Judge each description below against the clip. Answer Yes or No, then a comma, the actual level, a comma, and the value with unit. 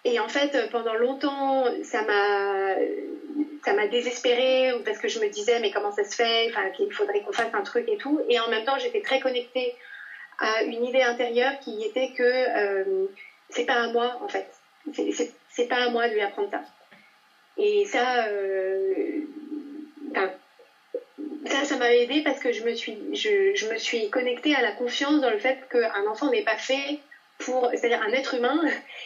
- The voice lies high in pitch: Yes, very high, 265 Hz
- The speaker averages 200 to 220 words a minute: No, average, 190 wpm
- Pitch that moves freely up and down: Yes, wide, 8.1 semitones